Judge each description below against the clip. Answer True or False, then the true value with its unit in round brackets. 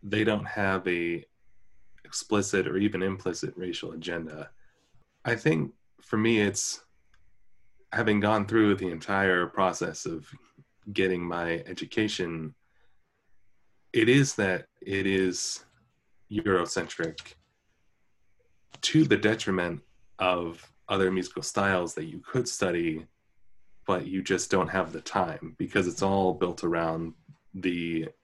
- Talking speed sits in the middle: False (115 wpm)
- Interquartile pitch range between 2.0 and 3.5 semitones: True (3.0 semitones)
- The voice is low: True (95 Hz)